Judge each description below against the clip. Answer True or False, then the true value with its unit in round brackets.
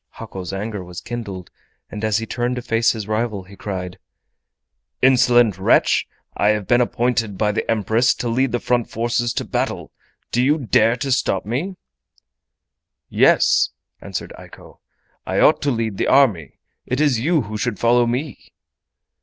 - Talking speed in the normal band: True (160 wpm)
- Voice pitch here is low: True (115 Hz)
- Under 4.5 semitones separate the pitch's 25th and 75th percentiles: True (2.9 semitones)